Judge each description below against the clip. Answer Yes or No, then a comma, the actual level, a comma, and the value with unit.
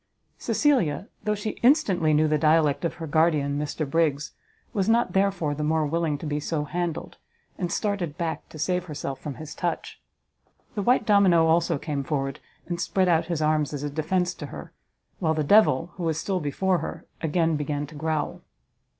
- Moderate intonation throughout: Yes, average, 3.3 semitones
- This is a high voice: No, medium, 160 Hz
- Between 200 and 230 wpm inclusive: No, average, 185 wpm